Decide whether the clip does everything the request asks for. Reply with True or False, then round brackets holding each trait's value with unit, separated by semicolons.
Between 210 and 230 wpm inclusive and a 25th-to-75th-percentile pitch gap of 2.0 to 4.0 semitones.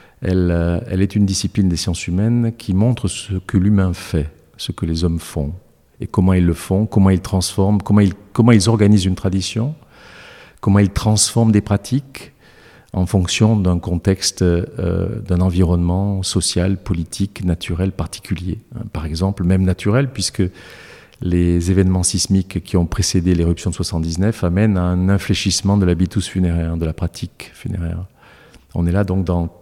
False (160 wpm; 2.6 semitones)